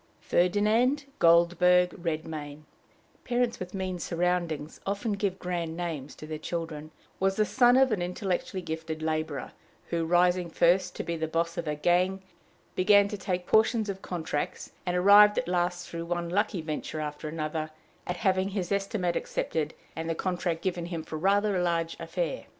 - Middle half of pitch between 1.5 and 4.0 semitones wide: Yes, average, 3.0 semitones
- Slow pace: No, average, 165 wpm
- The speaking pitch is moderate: Yes, medium, 175 Hz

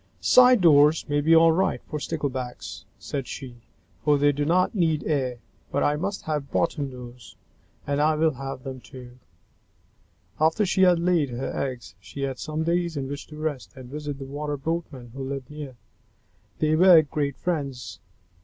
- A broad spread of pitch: No, average, 3.2 semitones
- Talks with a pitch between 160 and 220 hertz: No, medium, 145 Hz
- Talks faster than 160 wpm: Yes, average, 180 wpm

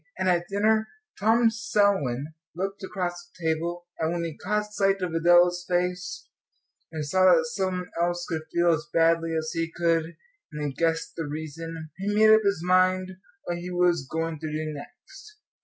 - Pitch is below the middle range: No, medium, 175 Hz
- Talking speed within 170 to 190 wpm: Yes, average, 180 wpm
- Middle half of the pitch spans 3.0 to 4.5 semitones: No, narrow, 2.6 semitones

